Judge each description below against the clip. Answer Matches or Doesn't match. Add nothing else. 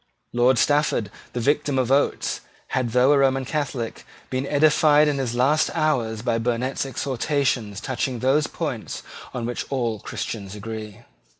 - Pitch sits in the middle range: Doesn't match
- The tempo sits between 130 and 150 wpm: Matches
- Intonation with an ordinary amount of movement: Matches